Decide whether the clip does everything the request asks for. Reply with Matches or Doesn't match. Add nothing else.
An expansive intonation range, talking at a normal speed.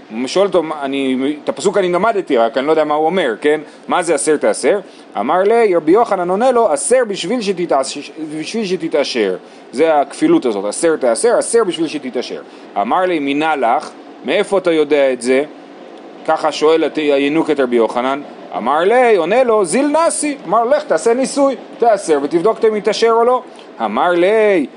Doesn't match